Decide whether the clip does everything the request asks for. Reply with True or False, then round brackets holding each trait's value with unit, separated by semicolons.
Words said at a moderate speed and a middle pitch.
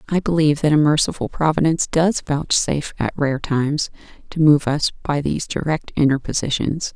True (155 wpm; 150 Hz)